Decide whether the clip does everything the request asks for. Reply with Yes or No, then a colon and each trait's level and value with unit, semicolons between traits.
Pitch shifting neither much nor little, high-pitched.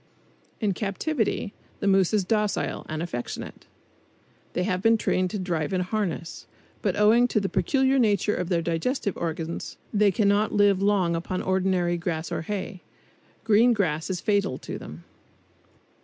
Yes: average, 3.4 semitones; high, 195 Hz